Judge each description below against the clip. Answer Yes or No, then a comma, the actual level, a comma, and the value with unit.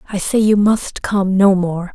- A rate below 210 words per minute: No, fast, 215 wpm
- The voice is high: Yes, high, 195 Hz